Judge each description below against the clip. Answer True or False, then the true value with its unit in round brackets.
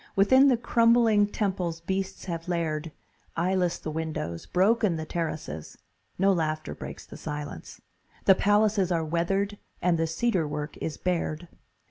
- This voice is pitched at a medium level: True (175 Hz)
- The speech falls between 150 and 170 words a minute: False (140 wpm)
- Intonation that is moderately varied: True (3.9 semitones)